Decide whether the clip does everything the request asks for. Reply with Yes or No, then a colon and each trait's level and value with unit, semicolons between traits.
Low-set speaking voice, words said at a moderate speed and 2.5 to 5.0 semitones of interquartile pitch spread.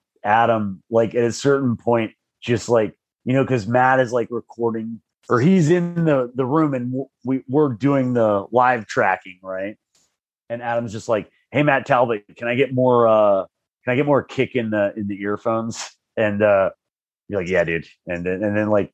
Yes: low, 120 Hz; average, 195 wpm; average, 3.3 semitones